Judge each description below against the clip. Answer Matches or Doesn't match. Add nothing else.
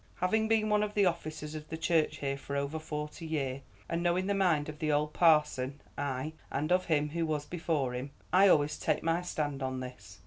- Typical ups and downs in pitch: Matches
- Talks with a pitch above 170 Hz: Doesn't match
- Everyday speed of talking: Doesn't match